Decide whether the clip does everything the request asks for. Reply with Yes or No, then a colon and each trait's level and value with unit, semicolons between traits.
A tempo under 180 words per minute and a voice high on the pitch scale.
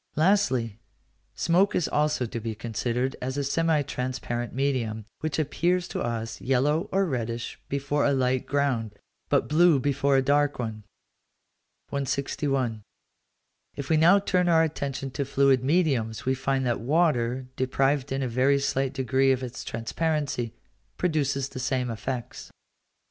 No: average, 145 wpm; low, 135 Hz